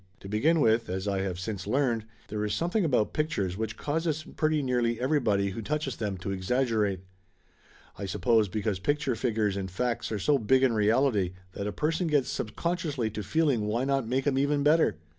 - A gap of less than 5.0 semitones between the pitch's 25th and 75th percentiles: No, wide, 5.6 semitones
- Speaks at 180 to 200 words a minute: Yes, average, 195 wpm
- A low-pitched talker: Yes, low, 115 Hz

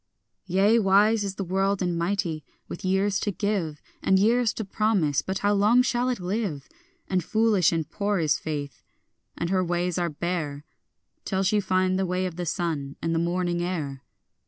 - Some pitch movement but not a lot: Yes, average, 3.2 semitones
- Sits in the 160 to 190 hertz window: Yes, medium, 185 Hz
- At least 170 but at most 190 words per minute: Yes, average, 185 wpm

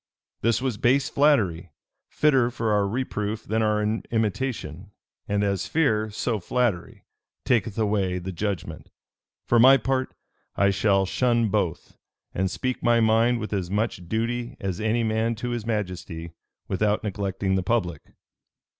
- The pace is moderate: Yes, average, 145 wpm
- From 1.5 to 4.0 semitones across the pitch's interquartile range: Yes, average, 3.4 semitones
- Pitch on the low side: Yes, low, 110 Hz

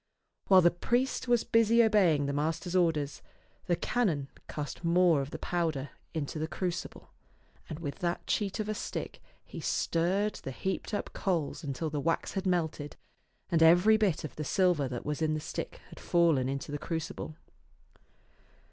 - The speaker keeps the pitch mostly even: No, average, 4.2 semitones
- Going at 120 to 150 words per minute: No, average, 170 wpm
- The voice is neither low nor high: Yes, medium, 165 Hz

